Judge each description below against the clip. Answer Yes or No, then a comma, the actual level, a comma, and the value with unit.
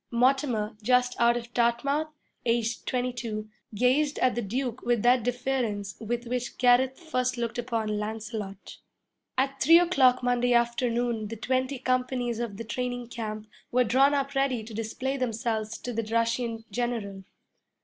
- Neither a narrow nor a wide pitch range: No, narrow, 2.0 semitones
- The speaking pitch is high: Yes, high, 240 Hz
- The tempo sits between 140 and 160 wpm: Yes, average, 150 wpm